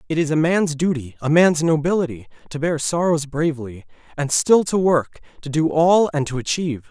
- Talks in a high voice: No, medium, 155 Hz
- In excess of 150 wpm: Yes, average, 190 wpm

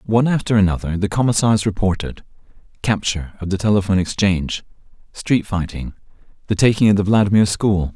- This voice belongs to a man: Yes, male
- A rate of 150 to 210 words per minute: No, slow, 135 wpm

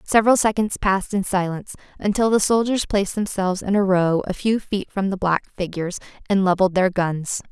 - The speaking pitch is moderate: No, high, 195 Hz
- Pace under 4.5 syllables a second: No, 5.8 syllables/s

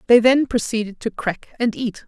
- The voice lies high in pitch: Yes, high, 230 Hz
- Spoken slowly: No, average, 200 wpm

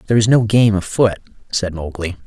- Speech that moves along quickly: No, average, 185 wpm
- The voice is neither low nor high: No, low, 105 Hz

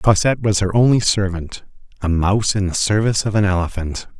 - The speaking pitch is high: No, low, 100 Hz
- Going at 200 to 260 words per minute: No, average, 185 wpm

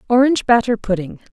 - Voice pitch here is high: Yes, high, 230 Hz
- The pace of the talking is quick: No, slow, 135 wpm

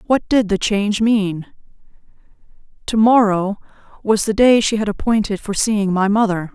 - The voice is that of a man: No, female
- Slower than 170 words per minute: Yes, average, 155 wpm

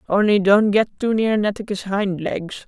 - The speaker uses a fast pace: No, average, 180 wpm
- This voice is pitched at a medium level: No, high, 205 Hz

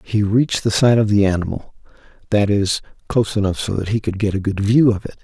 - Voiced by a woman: No, male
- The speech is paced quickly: Yes, fast, 240 wpm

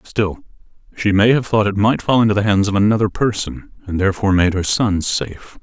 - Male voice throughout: Yes, male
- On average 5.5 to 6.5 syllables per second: Yes, 5.8 syllables/s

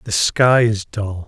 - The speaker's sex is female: No, male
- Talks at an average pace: Yes, average, 190 wpm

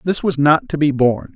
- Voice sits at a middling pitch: Yes, medium, 150 Hz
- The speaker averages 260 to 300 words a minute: Yes, fast, 265 wpm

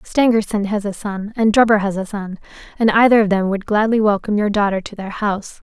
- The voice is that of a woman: Yes, female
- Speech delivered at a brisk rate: Yes, fast, 220 wpm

